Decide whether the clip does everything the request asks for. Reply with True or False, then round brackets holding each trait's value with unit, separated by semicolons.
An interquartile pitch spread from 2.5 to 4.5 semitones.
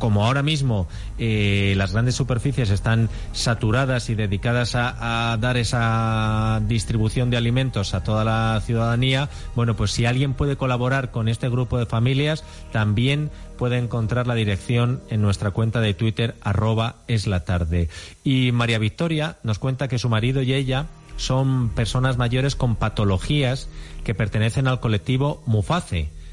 True (2.9 semitones)